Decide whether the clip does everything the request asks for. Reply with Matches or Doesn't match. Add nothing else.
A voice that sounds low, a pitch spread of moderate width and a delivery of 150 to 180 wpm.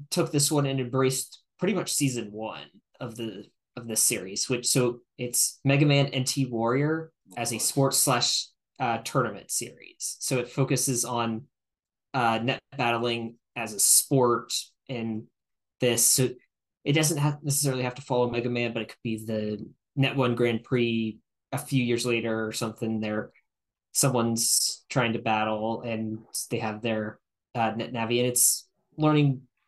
Matches